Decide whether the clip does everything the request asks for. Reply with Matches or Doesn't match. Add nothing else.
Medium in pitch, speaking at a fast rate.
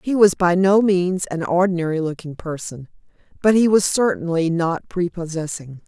Doesn't match